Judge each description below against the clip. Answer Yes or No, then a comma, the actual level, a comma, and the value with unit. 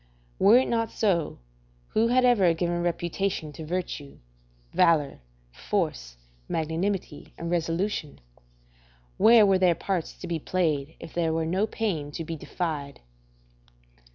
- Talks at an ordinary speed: No, slow, 130 wpm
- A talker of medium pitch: Yes, medium, 170 Hz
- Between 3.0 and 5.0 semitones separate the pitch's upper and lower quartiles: Yes, average, 3.6 semitones